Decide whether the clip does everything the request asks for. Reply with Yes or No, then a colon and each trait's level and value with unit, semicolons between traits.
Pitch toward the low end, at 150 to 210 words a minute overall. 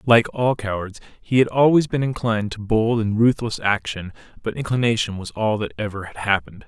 Yes: low, 110 Hz; average, 190 wpm